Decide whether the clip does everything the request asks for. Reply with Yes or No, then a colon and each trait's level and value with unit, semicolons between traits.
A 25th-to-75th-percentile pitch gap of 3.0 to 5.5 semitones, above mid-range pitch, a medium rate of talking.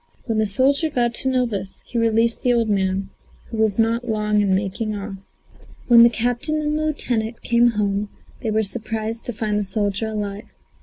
No: narrow, 2.4 semitones; high, 220 Hz; average, 190 wpm